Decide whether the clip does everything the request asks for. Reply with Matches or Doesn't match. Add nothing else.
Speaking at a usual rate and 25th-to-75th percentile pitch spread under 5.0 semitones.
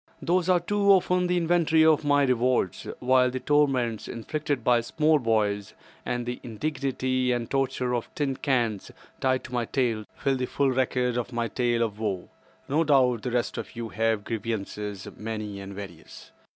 Matches